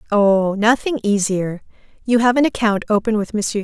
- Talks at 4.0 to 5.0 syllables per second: Yes, 4.7 syllables/s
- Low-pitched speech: No, high, 215 Hz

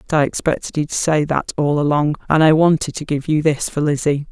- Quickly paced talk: Yes, fast, 235 wpm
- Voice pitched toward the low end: No, medium, 150 Hz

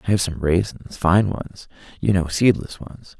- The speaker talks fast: No, average, 190 wpm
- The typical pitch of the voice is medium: No, very low, 95 Hz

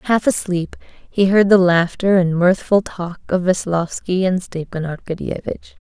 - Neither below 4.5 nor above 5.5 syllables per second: No, 4.3 syllables/s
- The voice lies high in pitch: No, medium, 180 Hz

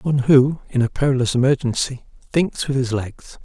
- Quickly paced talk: No, average, 175 wpm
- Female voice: No, male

